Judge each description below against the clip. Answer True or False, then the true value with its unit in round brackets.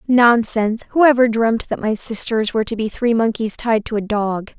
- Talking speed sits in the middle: False (210 wpm)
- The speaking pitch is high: True (225 Hz)